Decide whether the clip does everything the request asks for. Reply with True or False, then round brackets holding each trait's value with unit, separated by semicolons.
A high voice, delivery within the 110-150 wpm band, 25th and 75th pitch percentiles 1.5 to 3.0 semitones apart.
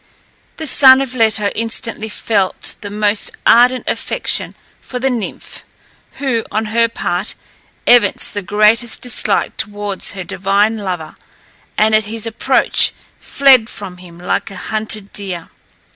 True (215 Hz; 135 wpm; 2.6 semitones)